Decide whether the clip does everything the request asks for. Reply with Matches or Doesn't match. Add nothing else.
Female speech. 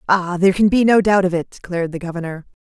Matches